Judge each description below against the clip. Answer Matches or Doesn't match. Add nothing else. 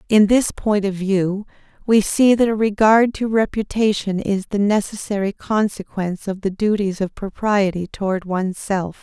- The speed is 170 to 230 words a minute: Doesn't match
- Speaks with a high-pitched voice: Matches